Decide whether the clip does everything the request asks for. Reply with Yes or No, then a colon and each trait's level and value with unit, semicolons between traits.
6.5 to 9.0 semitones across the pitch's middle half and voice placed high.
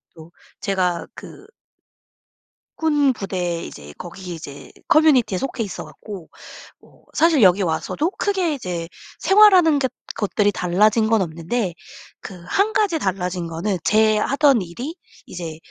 Yes: wide, 8.6 semitones; high, 210 Hz